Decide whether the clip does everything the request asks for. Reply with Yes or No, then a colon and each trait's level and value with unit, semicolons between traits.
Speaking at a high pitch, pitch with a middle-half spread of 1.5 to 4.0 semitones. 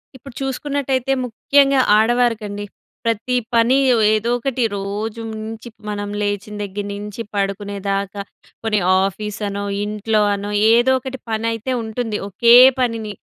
Yes: high, 220 Hz; average, 2.9 semitones